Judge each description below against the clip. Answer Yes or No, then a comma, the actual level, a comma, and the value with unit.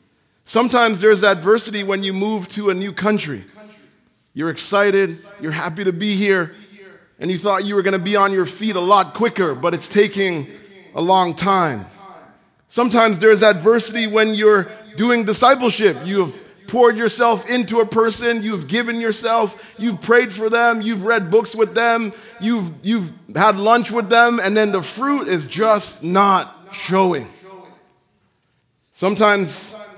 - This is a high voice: Yes, high, 205 Hz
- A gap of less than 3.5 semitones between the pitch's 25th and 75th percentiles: Yes, average, 2.9 semitones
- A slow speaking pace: No, average, 155 wpm